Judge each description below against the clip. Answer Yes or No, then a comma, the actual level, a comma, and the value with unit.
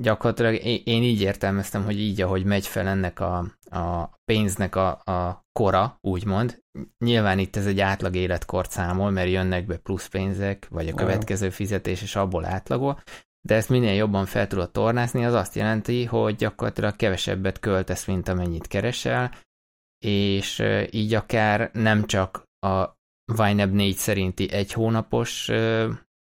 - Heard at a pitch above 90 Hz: Yes, low, 100 Hz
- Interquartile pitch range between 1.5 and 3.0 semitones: Yes, narrow, 2.6 semitones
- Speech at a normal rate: Yes, average, 145 wpm